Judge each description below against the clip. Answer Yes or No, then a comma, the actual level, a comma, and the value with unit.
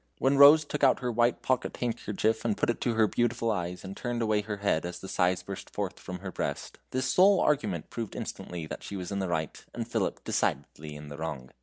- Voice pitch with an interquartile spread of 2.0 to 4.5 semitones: No, average, 5.2 semitones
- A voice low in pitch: Yes, low, 105 Hz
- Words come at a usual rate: No, fast, 225 wpm